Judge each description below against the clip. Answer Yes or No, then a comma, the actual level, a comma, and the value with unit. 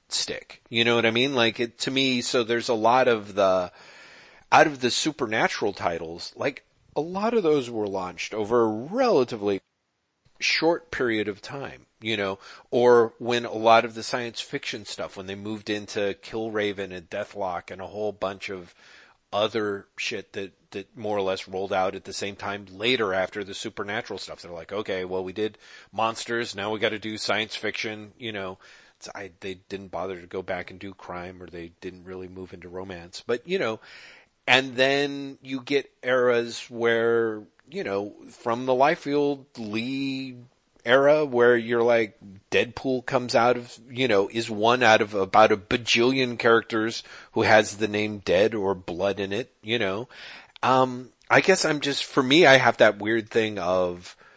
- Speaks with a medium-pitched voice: No, low, 110 Hz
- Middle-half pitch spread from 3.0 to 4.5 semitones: Yes, average, 3.8 semitones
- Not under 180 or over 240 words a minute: Yes, average, 185 wpm